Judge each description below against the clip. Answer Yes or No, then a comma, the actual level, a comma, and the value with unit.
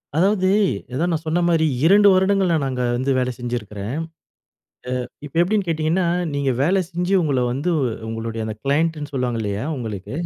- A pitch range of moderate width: No, wide, 6.1 semitones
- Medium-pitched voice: Yes, medium, 145 Hz